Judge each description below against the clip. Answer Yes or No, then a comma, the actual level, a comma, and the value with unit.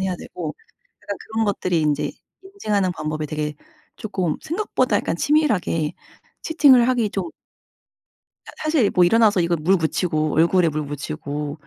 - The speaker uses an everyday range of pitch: No, wide, 6.2 semitones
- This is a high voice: No, medium, 180 Hz